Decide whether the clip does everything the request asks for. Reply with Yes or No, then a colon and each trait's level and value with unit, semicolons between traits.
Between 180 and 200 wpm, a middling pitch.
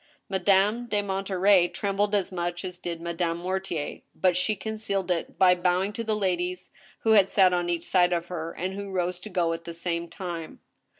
Yes: average, 195 wpm; medium, 180 Hz